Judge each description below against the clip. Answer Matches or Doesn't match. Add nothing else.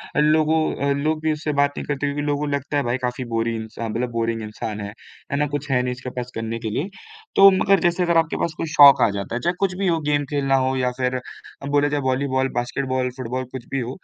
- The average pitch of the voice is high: Doesn't match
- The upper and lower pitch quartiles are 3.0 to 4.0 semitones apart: Matches